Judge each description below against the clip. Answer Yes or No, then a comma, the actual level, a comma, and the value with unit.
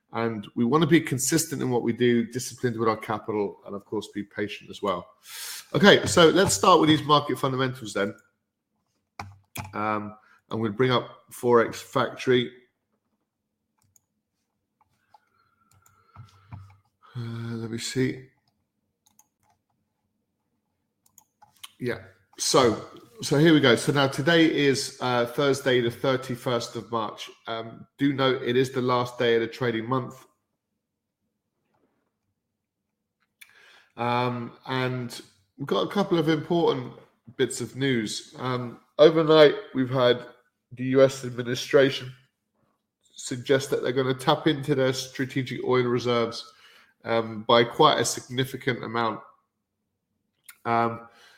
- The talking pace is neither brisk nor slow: No, slow, 125 wpm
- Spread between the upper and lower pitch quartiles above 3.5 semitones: No, narrow, 2.5 semitones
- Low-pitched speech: Yes, low, 125 Hz